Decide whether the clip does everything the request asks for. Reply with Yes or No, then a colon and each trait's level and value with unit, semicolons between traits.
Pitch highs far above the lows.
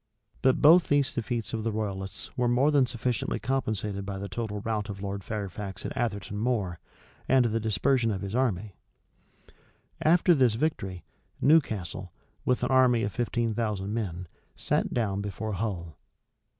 No: average, 3.9 semitones